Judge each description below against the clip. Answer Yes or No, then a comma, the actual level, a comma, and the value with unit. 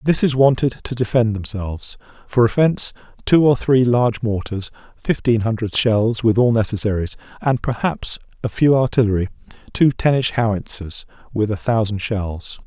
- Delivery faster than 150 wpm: No, average, 145 wpm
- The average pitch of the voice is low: Yes, low, 115 Hz